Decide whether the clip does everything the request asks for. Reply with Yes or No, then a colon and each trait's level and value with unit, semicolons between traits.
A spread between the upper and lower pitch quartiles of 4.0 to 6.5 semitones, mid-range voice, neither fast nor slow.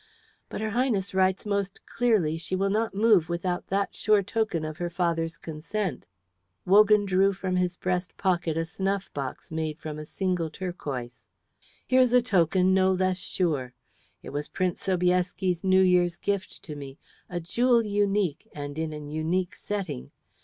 No: average, 3.3 semitones; medium, 180 Hz; average, 160 wpm